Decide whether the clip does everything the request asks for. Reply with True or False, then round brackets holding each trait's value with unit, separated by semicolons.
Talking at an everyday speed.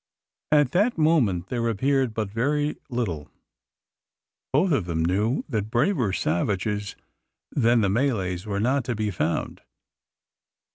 False (130 wpm)